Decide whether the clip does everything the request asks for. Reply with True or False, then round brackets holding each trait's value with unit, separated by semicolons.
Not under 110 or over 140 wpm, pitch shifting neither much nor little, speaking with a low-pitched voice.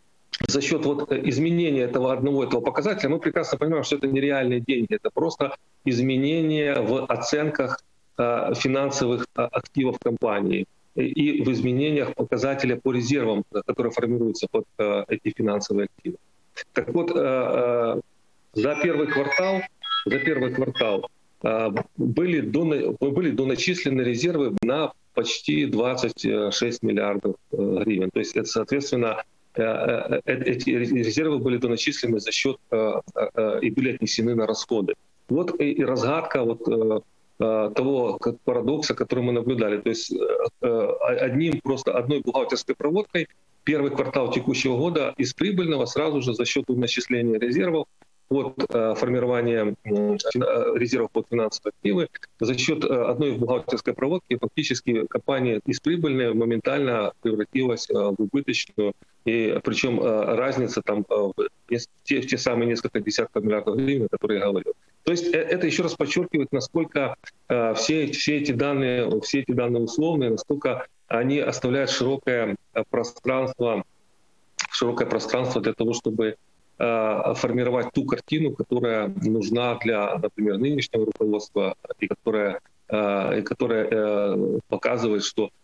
True (125 wpm; 4.2 semitones; 125 Hz)